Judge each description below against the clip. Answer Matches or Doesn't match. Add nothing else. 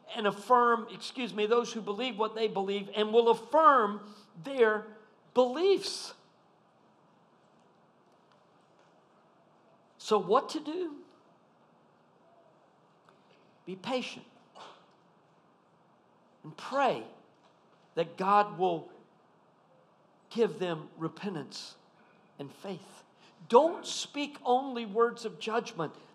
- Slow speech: Matches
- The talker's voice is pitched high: Matches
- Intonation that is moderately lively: Matches